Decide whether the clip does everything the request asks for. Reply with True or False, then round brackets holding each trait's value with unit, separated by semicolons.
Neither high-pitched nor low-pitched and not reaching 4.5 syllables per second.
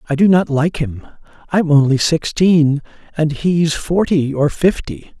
True (155 Hz; 3.9 syllables/s)